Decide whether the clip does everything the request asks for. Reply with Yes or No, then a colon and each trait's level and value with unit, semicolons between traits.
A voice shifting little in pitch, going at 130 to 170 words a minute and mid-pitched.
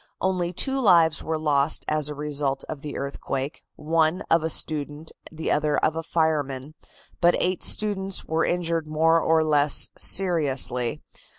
Yes: narrow, 2.3 semitones; average, 155 wpm; medium, 155 Hz